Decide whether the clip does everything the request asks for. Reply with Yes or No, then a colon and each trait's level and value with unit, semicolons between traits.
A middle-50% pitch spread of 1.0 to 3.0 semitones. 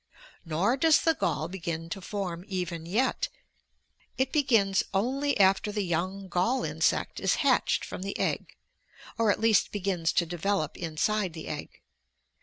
No: average, 4.2 semitones